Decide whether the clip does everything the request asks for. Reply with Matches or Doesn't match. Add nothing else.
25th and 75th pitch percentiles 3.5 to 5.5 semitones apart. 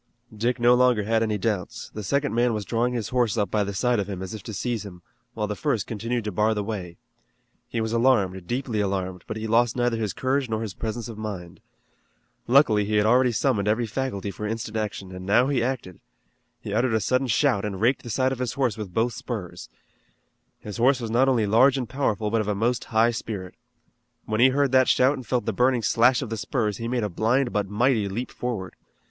Doesn't match